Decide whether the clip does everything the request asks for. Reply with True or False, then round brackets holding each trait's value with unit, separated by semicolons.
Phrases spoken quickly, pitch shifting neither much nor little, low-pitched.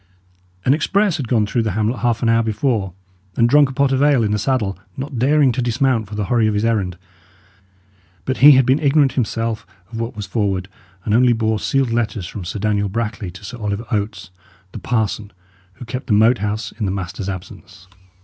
True (210 wpm; 3.7 semitones; 115 Hz)